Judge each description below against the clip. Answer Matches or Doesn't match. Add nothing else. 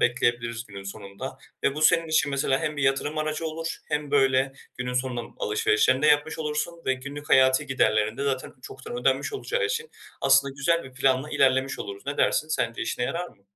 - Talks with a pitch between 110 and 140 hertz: Matches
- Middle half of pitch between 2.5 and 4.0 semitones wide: Matches